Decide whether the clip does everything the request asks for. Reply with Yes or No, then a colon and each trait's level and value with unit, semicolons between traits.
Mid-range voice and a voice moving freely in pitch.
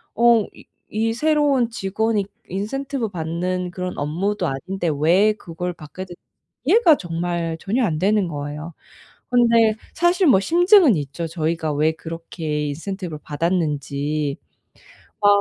Yes: medium, 180 Hz; wide, 5.9 semitones